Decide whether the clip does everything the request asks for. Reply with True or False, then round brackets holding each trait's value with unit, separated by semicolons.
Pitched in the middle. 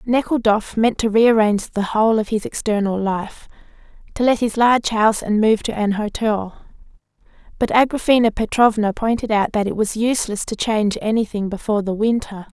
False (215 Hz)